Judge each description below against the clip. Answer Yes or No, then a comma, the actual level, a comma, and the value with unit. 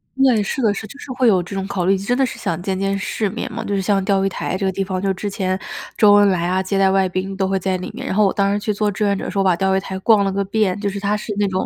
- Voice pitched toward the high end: Yes, high, 195 Hz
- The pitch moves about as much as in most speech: No, narrow, 1.5 semitones